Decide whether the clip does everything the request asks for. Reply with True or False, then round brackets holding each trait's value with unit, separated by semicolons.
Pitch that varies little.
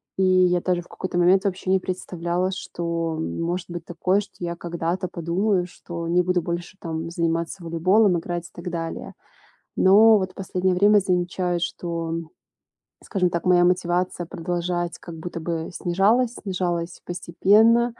True (1.7 semitones)